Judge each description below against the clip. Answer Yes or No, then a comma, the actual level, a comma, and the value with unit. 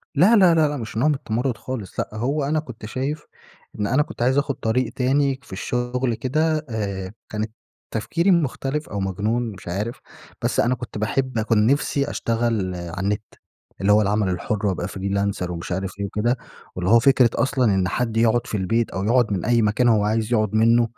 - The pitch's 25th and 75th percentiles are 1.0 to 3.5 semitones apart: No, average, 4.1 semitones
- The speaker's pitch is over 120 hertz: No, low, 115 Hz